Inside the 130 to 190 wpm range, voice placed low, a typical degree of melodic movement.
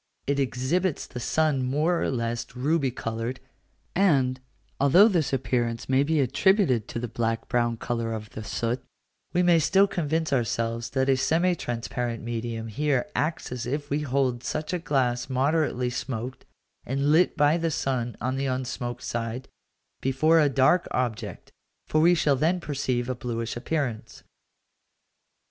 Yes: average, 155 wpm; low, 130 Hz; average, 4.2 semitones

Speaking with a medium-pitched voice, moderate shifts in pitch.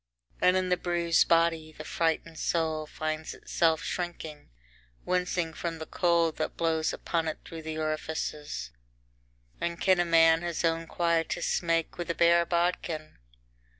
No: medium, 165 Hz; narrow, 1.4 semitones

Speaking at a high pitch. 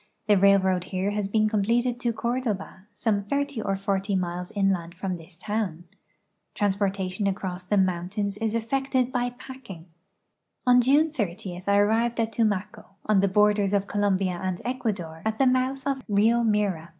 Yes: high, 205 Hz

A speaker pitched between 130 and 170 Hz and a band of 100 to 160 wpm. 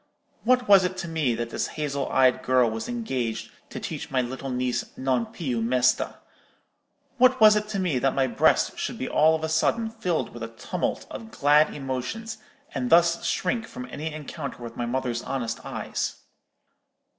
No: medium, 140 Hz; average, 180 wpm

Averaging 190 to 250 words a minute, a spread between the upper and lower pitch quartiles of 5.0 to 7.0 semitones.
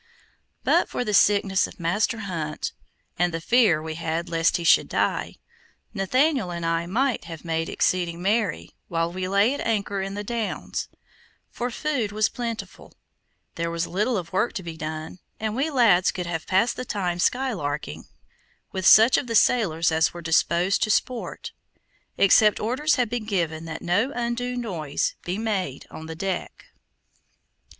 No: average, 165 wpm; average, 5.3 semitones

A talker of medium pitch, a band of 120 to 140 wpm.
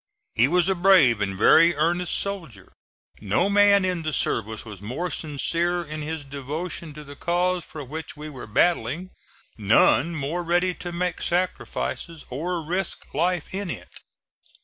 No: medium, 165 Hz; average, 155 wpm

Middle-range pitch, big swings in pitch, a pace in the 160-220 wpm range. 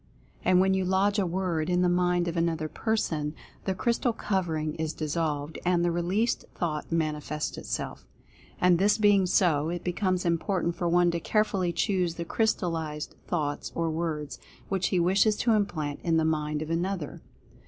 No: medium, 175 Hz; average, 3.0 semitones; average, 170 wpm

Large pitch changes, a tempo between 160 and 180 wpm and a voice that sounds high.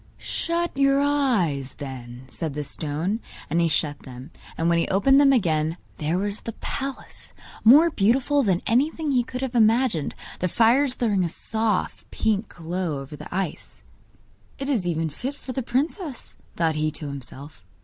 Yes: wide, 8.9 semitones; average, 170 wpm; high, 200 Hz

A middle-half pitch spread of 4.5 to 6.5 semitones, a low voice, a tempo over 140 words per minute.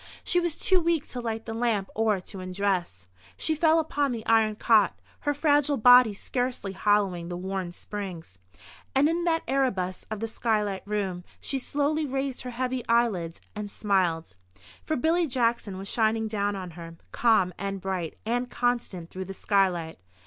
No: average, 5.1 semitones; high, 215 Hz; average, 170 wpm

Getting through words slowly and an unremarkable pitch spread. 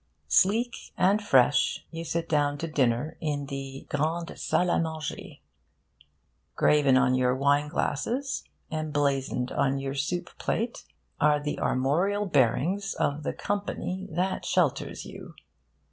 Yes: slow, 130 wpm; average, 4.5 semitones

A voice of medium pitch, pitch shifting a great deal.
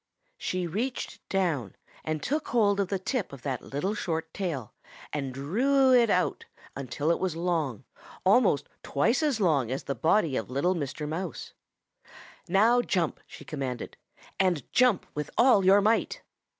Yes: medium, 175 Hz; wide, 6.7 semitones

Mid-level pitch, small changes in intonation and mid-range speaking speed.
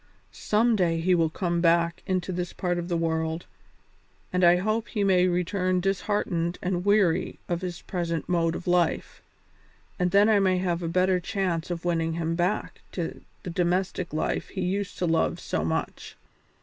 Yes: medium, 180 Hz; narrow, 1.8 semitones; average, 175 wpm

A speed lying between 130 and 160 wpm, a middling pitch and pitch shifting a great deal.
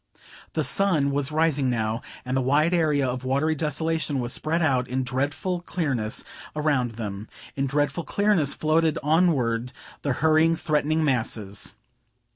No: average, 140 wpm; medium, 145 Hz; average, 3.8 semitones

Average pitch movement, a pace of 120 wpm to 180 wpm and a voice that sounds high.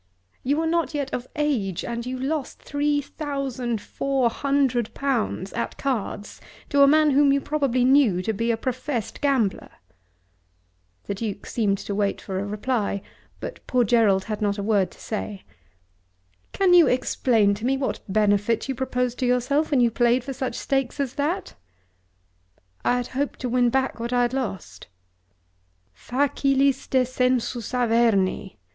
Yes: average, 4.0 semitones; average, 160 wpm; very high, 250 Hz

